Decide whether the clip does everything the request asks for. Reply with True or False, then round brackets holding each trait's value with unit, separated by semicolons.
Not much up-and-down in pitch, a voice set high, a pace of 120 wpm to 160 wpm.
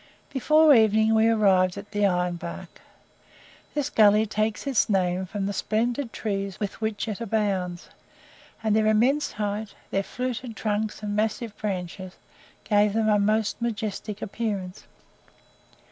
True (1.9 semitones; 210 Hz; 140 wpm)